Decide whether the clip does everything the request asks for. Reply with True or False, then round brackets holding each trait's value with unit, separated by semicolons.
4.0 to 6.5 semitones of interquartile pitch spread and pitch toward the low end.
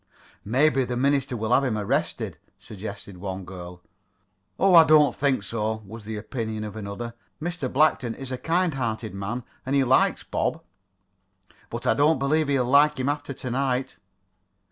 True (4.6 semitones; 125 Hz)